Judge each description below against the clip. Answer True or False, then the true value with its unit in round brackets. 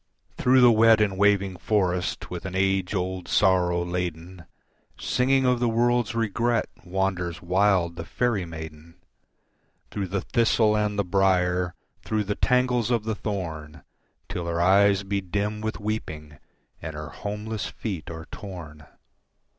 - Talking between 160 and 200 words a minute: False (145 wpm)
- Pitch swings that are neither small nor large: True (3.6 semitones)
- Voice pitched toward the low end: True (95 Hz)